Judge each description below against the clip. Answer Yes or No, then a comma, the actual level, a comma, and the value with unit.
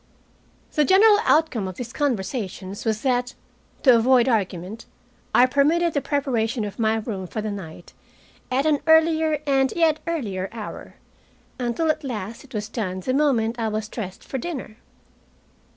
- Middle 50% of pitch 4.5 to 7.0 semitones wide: Yes, average, 5.2 semitones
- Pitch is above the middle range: Yes, high, 245 Hz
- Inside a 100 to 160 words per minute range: Yes, average, 155 wpm